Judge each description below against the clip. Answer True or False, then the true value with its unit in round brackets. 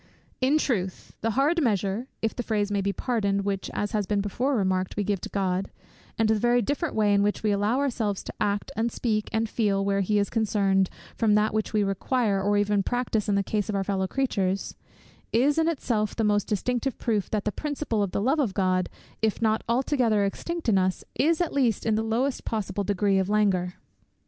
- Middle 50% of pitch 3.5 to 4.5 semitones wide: False (3.1 semitones)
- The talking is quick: True (215 wpm)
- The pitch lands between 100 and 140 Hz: False (210 Hz)